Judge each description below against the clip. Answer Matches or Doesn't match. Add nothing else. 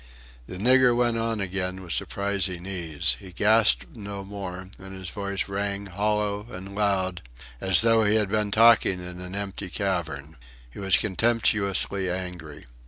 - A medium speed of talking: Matches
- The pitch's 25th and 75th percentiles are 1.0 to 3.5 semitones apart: Matches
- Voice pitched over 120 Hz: Doesn't match